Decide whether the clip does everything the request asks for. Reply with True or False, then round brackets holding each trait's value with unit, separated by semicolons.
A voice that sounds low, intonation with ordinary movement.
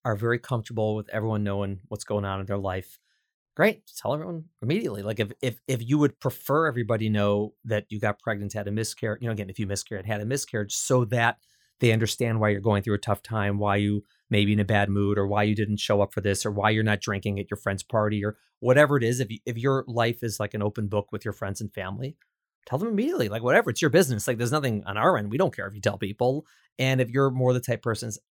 True (110 Hz; 3.1 semitones)